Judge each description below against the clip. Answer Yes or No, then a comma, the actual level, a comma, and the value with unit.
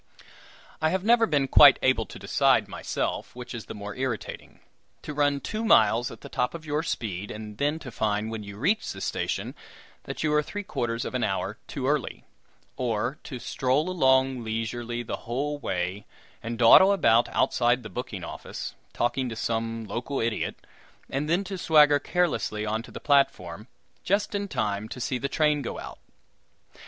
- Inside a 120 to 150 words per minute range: No, average, 180 wpm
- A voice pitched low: Yes, low, 125 Hz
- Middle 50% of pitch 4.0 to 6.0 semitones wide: Yes, average, 5.1 semitones